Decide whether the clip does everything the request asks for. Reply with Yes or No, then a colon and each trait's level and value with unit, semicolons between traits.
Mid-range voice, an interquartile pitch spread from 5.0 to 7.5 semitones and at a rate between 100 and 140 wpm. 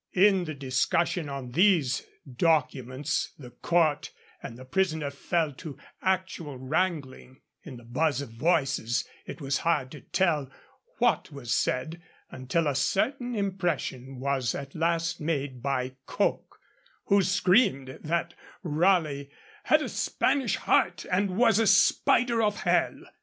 Yes: medium, 155 Hz; wide, 5.5 semitones; slow, 135 wpm